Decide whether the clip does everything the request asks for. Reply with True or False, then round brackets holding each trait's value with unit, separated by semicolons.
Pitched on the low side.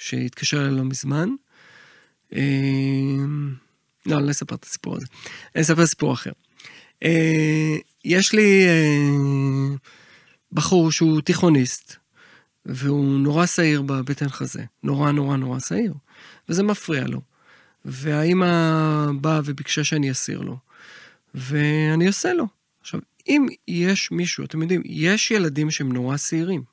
False (150 Hz)